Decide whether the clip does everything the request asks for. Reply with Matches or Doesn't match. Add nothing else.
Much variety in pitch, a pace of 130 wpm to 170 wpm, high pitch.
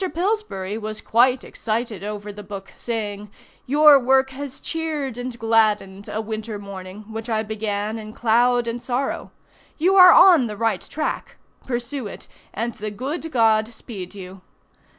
Doesn't match